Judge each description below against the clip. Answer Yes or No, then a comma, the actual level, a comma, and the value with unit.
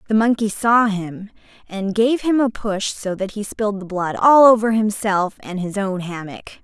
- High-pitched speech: Yes, high, 205 Hz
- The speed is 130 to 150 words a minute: No, average, 200 wpm